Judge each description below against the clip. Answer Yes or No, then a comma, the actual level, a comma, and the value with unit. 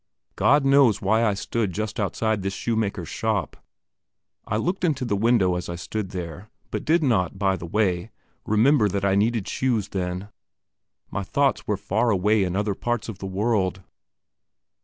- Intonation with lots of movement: No, average, 3.3 semitones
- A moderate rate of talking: Yes, average, 170 wpm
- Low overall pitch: Yes, low, 105 Hz